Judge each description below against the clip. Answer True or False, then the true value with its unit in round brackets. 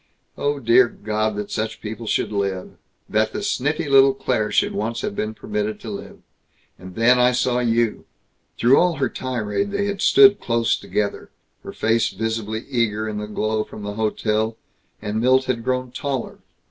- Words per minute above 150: True (175 wpm)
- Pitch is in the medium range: False (115 Hz)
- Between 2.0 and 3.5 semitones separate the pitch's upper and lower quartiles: True (3.1 semitones)